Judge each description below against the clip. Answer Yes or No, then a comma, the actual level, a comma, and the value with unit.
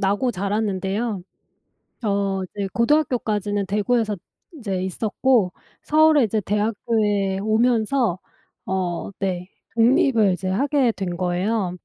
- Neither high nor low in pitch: No, high, 205 Hz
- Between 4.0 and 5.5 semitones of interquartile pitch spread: No, average, 3.4 semitones